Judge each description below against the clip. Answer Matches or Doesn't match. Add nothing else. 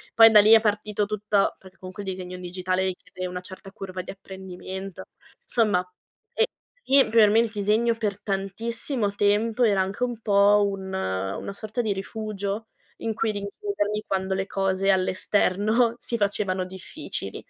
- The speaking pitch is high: Matches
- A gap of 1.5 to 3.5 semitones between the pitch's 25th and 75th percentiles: Matches